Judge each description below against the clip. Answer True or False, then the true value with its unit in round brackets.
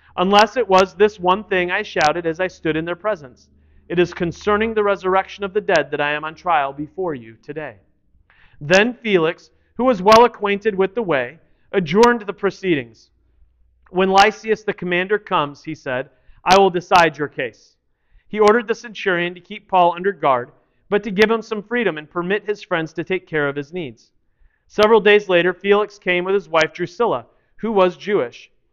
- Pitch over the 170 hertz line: True (185 Hz)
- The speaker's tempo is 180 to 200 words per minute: True (190 wpm)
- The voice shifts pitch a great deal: False (4.7 semitones)